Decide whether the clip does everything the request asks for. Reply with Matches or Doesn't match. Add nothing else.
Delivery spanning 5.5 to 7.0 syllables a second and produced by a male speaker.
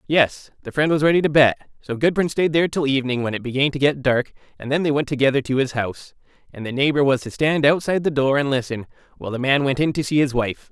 Matches